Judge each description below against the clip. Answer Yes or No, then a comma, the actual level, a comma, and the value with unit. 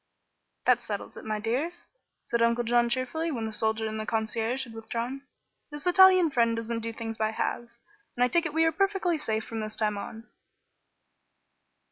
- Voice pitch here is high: Yes, high, 235 Hz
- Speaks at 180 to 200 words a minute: Yes, average, 185 wpm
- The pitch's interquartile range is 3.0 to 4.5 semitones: No, average, 5.0 semitones